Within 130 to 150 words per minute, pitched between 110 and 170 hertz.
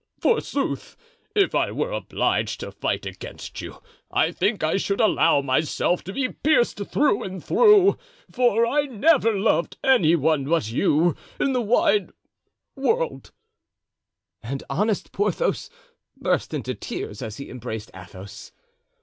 No: slow, 135 wpm; high, 200 Hz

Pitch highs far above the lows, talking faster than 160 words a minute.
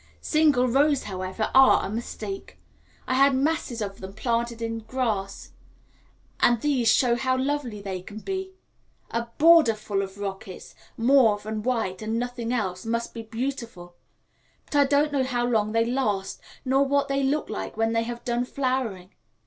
No: average, 3.8 semitones; average, 170 wpm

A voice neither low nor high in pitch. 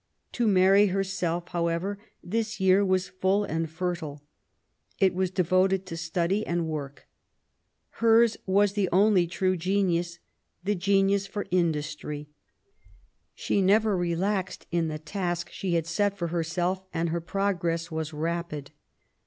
Yes: medium, 180 Hz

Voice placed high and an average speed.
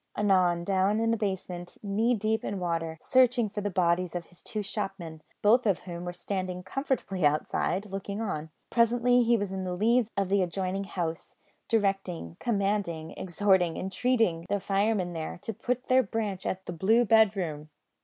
Yes: high, 195 Hz; average, 170 wpm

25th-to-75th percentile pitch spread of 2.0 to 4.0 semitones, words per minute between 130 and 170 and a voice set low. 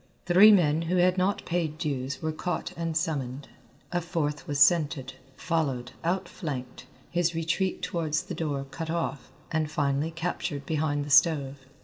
No: average, 3.0 semitones; average, 150 wpm; medium, 160 Hz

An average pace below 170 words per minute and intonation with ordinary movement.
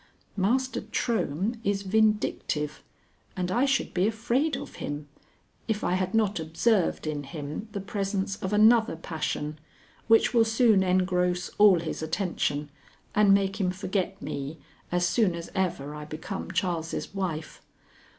Yes: average, 140 wpm; average, 4.6 semitones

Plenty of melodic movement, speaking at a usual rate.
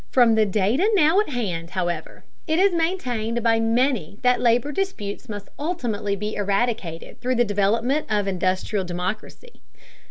No: average, 4.7 semitones; average, 150 wpm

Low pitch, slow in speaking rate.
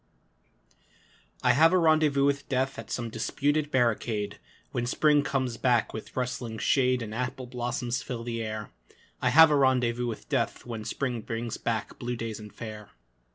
No: low, 125 Hz; average, 165 wpm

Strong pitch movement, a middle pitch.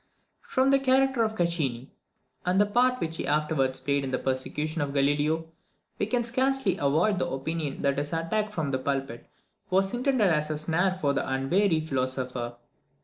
Yes: wide, 6.9 semitones; medium, 160 Hz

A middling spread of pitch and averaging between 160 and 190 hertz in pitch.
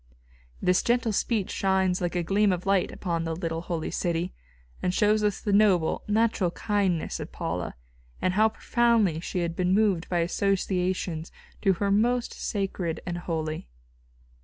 Yes: average, 3.1 semitones; medium, 185 Hz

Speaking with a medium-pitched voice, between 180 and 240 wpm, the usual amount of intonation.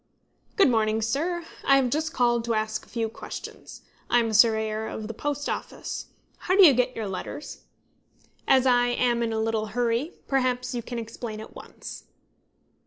No: high, 240 Hz; average, 185 wpm; average, 3.0 semitones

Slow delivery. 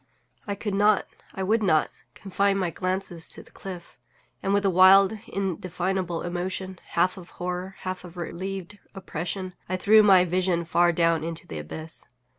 No: average, 170 wpm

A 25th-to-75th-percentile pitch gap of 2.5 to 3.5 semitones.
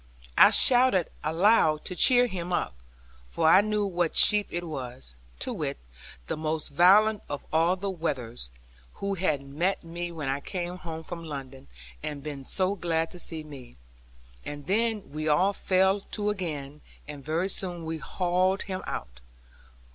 No: average, 4.2 semitones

